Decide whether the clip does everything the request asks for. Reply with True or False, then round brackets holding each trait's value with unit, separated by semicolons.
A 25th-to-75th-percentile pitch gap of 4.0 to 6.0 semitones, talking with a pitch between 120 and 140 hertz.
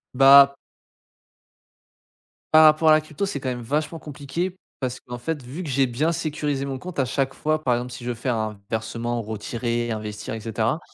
True (4.4 semitones; 135 Hz)